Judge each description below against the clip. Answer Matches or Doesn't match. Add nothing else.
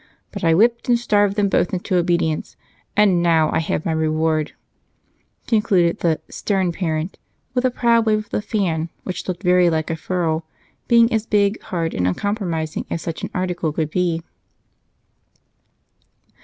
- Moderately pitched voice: Matches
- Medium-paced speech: Matches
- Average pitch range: Matches